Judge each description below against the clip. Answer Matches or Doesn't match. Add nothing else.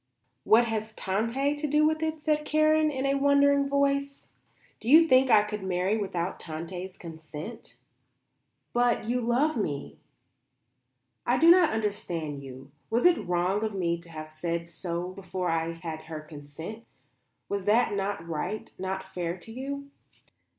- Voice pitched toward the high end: Matches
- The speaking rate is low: Doesn't match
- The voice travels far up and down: Matches